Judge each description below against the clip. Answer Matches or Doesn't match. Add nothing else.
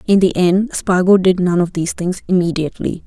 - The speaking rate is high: Doesn't match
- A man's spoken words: Doesn't match